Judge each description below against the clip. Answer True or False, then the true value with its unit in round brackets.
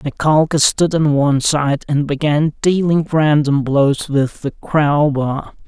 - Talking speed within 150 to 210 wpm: False (135 wpm)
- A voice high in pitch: False (145 Hz)